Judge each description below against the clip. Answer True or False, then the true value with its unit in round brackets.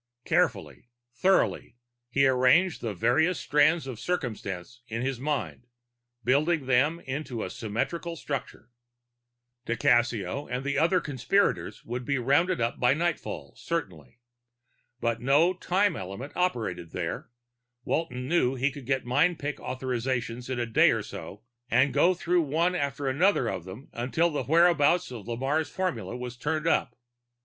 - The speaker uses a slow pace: False (145 wpm)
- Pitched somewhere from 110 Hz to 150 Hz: True (135 Hz)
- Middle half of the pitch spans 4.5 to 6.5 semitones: True (5.1 semitones)